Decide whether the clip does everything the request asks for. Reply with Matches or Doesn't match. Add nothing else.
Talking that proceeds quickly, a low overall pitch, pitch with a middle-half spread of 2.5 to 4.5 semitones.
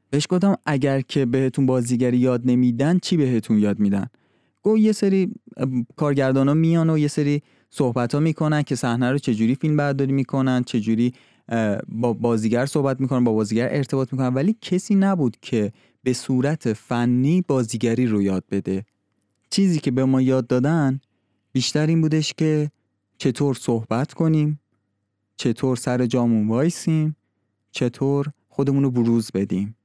Doesn't match